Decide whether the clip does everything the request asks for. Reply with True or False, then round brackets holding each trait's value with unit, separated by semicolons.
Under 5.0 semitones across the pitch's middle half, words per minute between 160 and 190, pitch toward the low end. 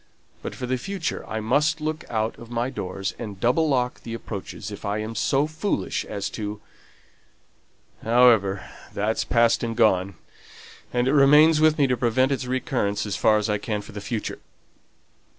True (4.3 semitones; 175 wpm; 120 Hz)